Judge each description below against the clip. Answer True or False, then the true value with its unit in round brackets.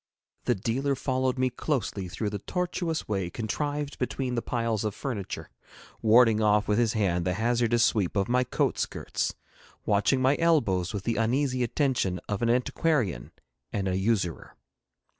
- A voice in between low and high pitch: False (115 Hz)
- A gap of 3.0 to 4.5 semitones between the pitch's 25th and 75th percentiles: True (4.0 semitones)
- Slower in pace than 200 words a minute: True (160 wpm)